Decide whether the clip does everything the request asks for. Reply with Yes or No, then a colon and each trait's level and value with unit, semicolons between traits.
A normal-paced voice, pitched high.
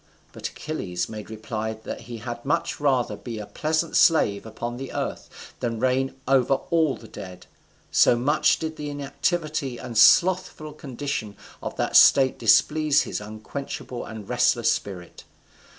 No: average, 150 wpm; low, 125 Hz